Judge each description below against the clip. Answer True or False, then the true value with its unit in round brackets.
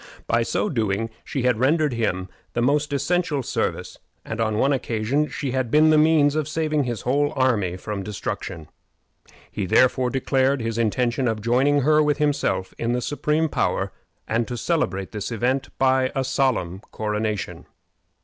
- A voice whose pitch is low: True (130 Hz)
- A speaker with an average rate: True (165 wpm)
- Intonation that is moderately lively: True (4.4 semitones)